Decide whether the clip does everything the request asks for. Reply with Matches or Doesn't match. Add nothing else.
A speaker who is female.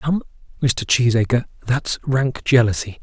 Doesn't match